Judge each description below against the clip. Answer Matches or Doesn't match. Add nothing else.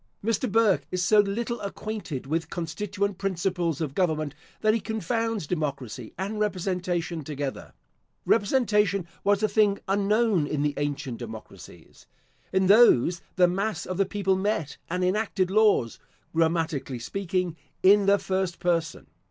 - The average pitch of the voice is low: Doesn't match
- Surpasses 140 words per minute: Doesn't match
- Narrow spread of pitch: Doesn't match